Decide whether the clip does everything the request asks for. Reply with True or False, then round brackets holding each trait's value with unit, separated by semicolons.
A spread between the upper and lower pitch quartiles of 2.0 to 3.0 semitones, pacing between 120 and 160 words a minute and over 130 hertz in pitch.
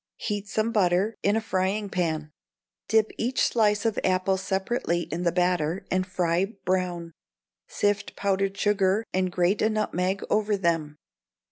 True (2.6 semitones; 145 wpm; 190 Hz)